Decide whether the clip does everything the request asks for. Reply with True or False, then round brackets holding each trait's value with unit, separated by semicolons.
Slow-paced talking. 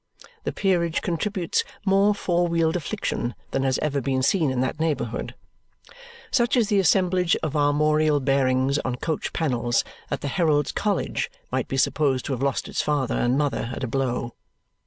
False (170 wpm)